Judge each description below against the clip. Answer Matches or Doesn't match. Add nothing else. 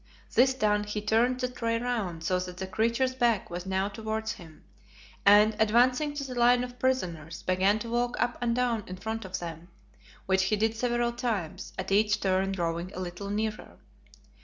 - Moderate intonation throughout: Matches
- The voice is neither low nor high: Doesn't match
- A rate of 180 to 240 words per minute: Matches